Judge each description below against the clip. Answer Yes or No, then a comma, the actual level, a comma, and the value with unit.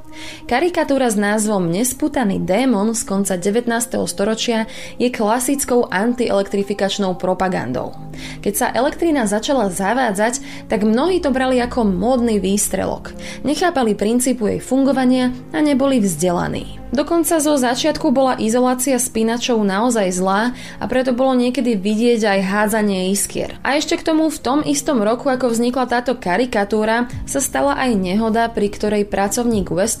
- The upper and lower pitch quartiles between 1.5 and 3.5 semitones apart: No, average, 4.3 semitones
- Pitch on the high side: Yes, high, 235 Hz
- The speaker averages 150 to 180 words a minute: No, average, 135 wpm